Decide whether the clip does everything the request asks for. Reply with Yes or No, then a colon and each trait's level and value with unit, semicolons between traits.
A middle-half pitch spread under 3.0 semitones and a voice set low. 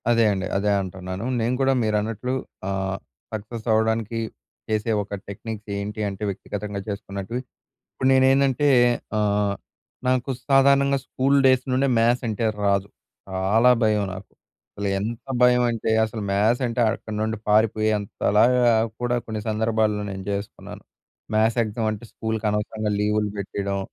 Yes: narrow, 2.6 semitones; low, 110 Hz